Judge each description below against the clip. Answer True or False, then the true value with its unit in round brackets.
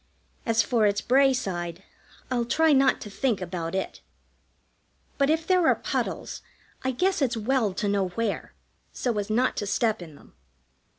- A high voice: True (225 Hz)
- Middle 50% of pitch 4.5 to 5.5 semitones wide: True (5.0 semitones)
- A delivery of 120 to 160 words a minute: False (170 wpm)